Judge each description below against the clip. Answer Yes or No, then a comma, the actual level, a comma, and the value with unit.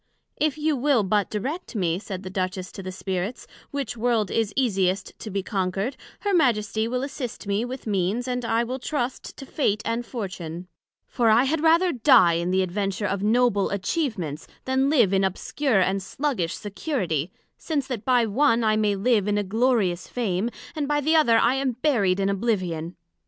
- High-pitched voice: Yes, high, 220 Hz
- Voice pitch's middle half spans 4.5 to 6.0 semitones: Yes, average, 5.2 semitones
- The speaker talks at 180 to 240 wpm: Yes, average, 185 wpm